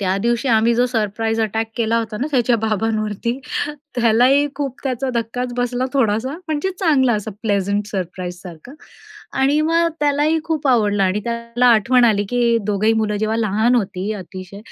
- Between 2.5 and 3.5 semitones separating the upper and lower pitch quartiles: Yes, average, 3.2 semitones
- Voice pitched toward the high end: Yes, high, 230 Hz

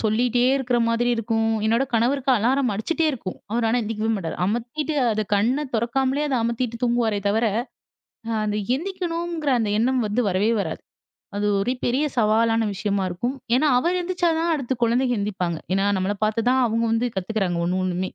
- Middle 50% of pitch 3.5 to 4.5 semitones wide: Yes, average, 3.8 semitones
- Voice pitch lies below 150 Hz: No, high, 230 Hz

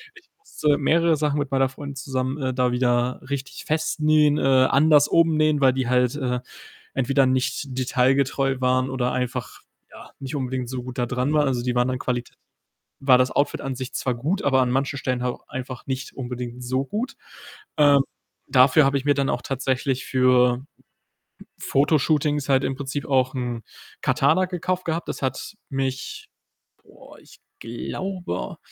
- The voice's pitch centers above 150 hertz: No, low, 135 Hz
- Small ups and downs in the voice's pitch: Yes, narrow, 2.3 semitones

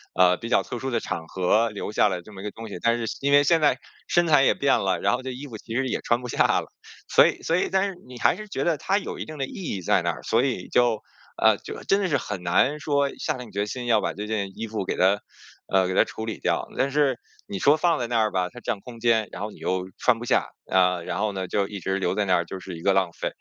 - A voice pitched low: Yes, low, 115 Hz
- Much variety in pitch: Yes, wide, 5.7 semitones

